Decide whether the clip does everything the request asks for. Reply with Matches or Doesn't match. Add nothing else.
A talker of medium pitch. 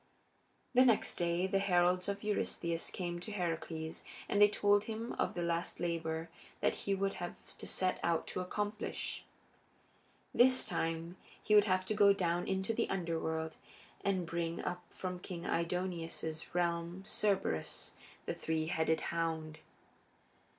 Matches